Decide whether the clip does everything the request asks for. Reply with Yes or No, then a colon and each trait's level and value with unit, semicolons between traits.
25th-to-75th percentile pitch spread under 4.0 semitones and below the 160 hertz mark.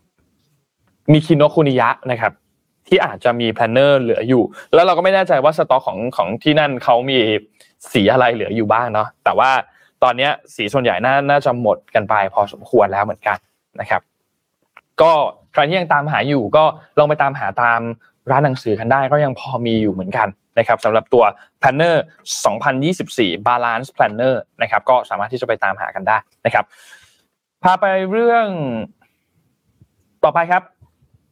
No: average, 4.8 semitones; low, 135 Hz